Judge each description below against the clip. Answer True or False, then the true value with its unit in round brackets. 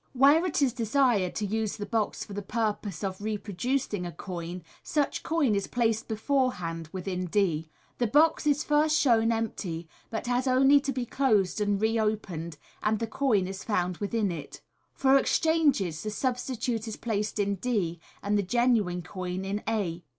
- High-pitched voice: True (215 Hz)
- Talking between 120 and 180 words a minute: True (170 wpm)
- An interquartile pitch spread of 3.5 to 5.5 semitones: True (4.9 semitones)